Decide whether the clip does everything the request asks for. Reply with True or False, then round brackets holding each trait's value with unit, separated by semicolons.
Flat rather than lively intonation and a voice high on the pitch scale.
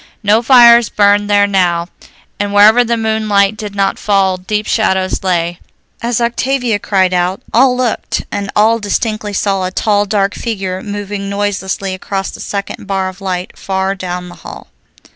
True (2.2 semitones; 200 Hz)